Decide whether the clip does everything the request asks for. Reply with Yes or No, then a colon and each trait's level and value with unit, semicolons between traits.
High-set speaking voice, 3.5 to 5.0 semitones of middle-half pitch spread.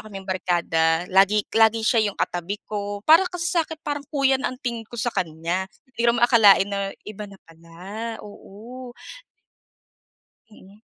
Yes: high, 210 Hz; average, 4.1 semitones